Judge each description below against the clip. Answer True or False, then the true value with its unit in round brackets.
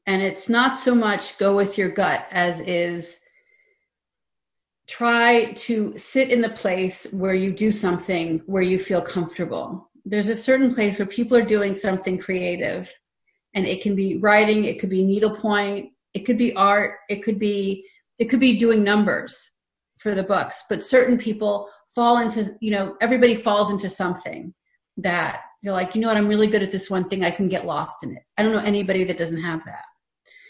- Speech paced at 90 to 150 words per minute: False (190 wpm)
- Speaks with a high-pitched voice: True (205 Hz)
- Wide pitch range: False (3.3 semitones)